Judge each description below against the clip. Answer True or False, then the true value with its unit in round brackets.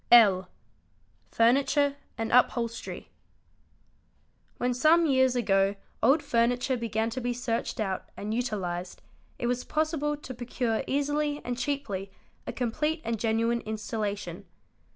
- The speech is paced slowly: True (130 wpm)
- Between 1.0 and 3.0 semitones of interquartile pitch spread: False (3.8 semitones)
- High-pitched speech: True (240 Hz)